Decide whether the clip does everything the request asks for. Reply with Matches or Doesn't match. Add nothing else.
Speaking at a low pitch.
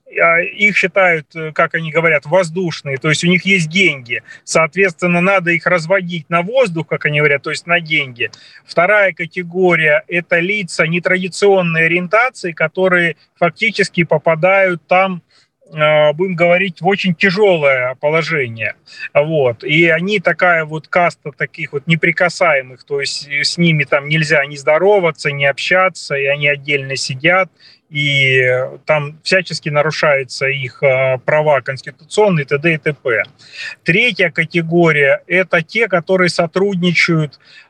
Doesn't match